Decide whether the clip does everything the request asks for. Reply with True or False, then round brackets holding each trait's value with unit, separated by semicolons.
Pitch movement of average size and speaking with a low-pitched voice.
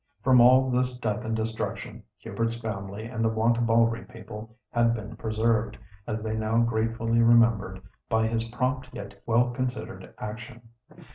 False (1.3 semitones; 115 Hz)